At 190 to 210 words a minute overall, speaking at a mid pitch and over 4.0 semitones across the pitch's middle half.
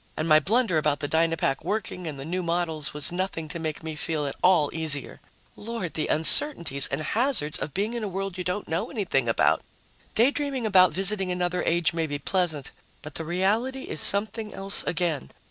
Yes: average, 195 wpm; medium, 175 Hz; average, 4.4 semitones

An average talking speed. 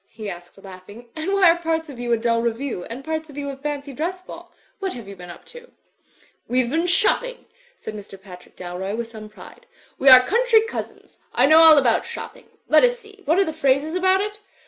No: fast, 220 wpm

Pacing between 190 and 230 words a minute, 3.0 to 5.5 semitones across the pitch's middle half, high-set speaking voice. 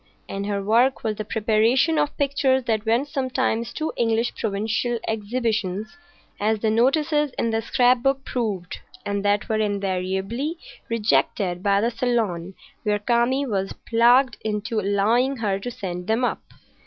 No: average, 150 wpm; average, 3.6 semitones; high, 225 Hz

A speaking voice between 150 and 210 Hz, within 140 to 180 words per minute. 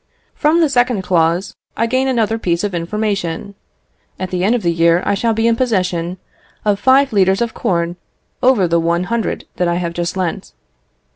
No: high, 190 Hz; average, 190 wpm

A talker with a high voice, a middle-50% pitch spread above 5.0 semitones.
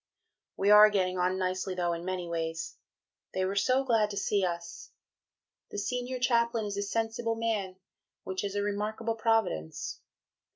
No: high, 205 Hz; average, 3.4 semitones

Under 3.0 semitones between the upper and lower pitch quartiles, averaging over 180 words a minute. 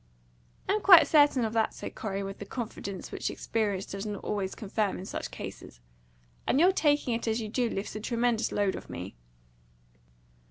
No: average, 3.6 semitones; average, 190 wpm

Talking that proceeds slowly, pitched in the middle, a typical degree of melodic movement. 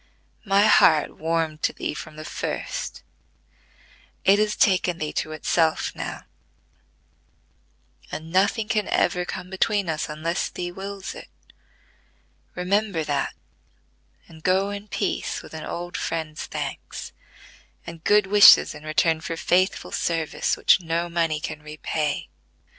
Yes: slow, 130 wpm; medium, 170 Hz; average, 3.6 semitones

